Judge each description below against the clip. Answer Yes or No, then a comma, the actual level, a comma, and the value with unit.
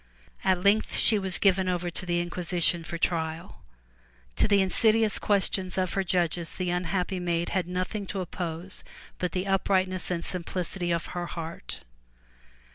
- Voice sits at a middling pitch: Yes, medium, 180 Hz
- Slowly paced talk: No, average, 155 wpm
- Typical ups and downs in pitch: No, narrow, 1.7 semitones